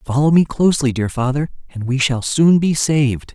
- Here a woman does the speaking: No, male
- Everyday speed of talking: Yes, average, 195 wpm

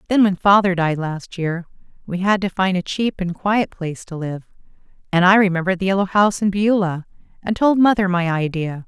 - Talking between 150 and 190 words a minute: No, fast, 205 wpm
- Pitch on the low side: No, medium, 185 Hz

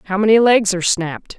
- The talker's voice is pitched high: Yes, high, 200 Hz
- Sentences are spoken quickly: Yes, fast, 215 wpm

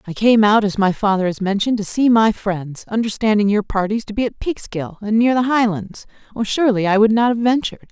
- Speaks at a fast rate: Yes, fast, 225 wpm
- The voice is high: Yes, high, 215 Hz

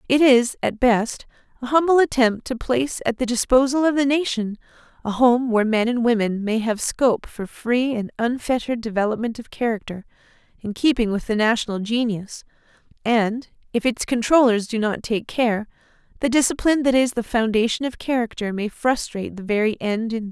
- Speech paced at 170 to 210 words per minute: Yes, average, 175 wpm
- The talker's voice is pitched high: Yes, high, 235 Hz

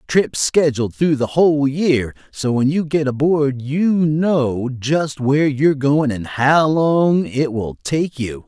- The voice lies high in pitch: No, medium, 140 Hz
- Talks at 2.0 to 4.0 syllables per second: Yes, 3.7 syllables/s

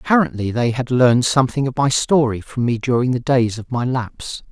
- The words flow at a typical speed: No, fast, 215 wpm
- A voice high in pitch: No, low, 125 Hz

